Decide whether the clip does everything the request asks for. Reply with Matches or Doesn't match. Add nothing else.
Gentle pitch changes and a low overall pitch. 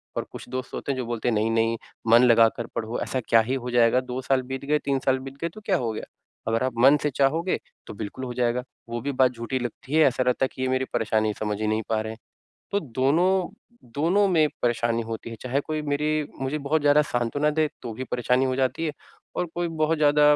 Doesn't match